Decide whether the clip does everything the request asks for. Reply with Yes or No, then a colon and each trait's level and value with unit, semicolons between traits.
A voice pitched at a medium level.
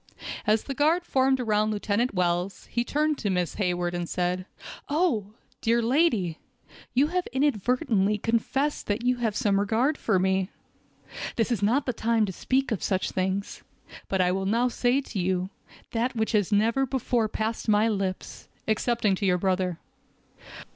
No: high, 220 Hz